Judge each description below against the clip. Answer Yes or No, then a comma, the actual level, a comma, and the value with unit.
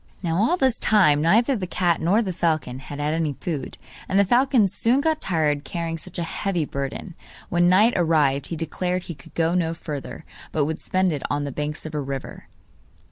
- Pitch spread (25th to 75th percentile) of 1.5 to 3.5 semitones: No, average, 4.1 semitones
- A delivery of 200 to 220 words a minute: Yes, fast, 205 wpm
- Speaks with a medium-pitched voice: Yes, medium, 165 Hz